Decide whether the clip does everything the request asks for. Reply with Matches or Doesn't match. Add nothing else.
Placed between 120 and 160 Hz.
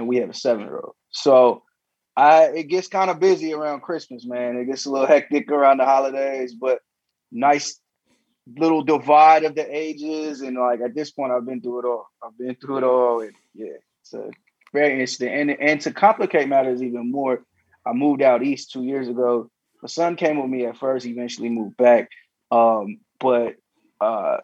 Matches